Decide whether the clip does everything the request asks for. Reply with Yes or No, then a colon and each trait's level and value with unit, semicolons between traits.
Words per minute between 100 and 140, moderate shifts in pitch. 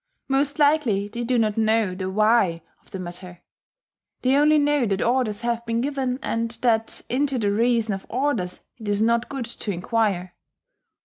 No: average, 175 wpm; average, 4.0 semitones